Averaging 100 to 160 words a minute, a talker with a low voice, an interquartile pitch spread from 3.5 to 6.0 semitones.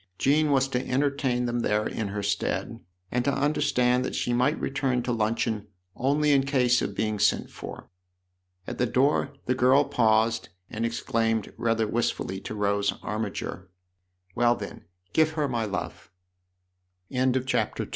No: average, 170 wpm; low, 120 Hz; average, 3.8 semitones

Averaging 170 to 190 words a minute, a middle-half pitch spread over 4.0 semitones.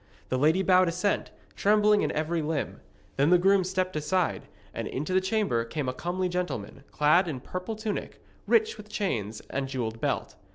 Yes: average, 175 wpm; average, 5.1 semitones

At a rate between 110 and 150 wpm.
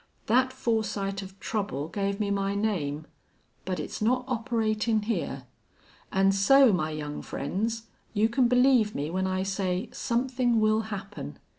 Yes: average, 145 wpm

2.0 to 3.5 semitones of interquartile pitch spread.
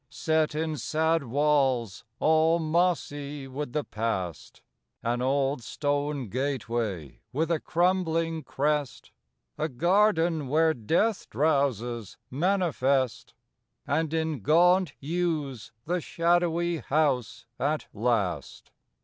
No: average, 4.3 semitones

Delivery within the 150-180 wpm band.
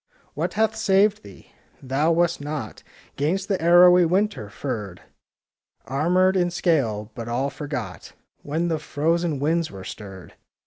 No: slow, 135 wpm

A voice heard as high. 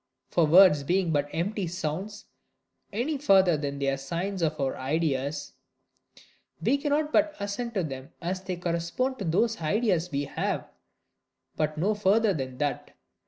No: medium, 175 Hz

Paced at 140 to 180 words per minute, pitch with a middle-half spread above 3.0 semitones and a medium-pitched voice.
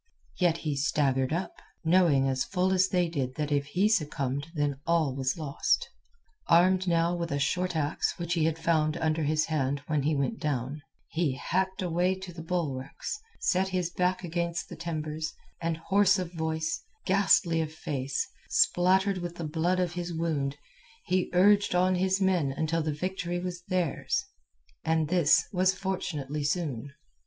Yes: average, 165 wpm; average, 3.4 semitones; medium, 165 Hz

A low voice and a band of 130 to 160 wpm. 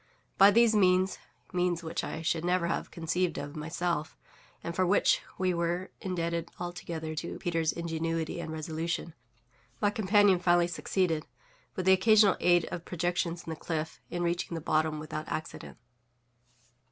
No: medium, 170 Hz; average, 150 wpm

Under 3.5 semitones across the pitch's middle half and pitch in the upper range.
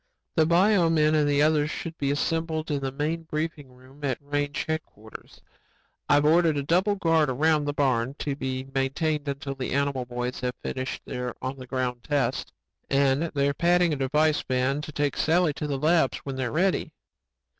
No: average, 3.0 semitones; medium, 145 Hz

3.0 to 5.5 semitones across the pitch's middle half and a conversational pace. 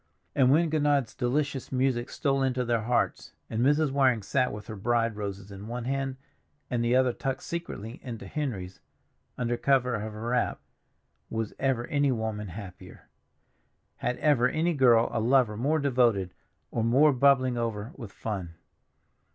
Yes: average, 3.5 semitones; average, 160 wpm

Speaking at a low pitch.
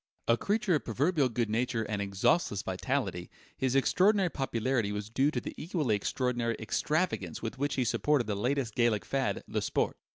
Yes: low, 125 Hz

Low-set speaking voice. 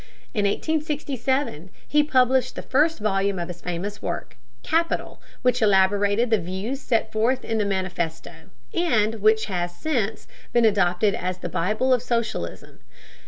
No: high, 215 Hz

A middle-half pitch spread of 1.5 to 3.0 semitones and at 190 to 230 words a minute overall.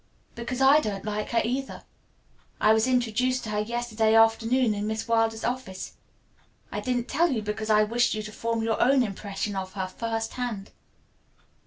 No: narrow, 2.4 semitones; average, 175 wpm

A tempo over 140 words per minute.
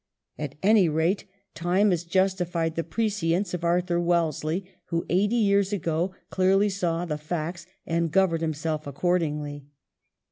No: slow, 135 wpm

